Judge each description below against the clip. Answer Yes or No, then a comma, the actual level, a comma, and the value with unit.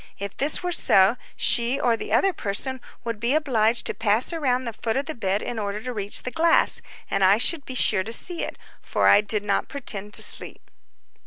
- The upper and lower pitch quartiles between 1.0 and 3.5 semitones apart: No, average, 4.5 semitones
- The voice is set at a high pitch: Yes, high, 230 Hz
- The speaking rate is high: Yes, fast, 220 wpm